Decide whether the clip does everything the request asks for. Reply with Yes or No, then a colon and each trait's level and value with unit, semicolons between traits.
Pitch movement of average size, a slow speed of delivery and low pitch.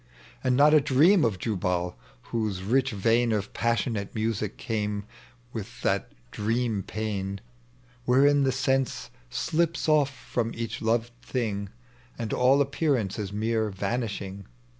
Yes: average, 4.2 semitones; slow, 130 wpm; low, 115 Hz